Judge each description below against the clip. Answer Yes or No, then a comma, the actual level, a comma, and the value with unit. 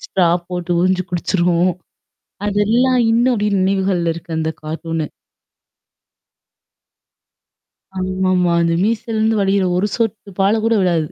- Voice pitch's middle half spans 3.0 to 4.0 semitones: Yes, average, 3.4 semitones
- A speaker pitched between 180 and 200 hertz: Yes, high, 190 Hz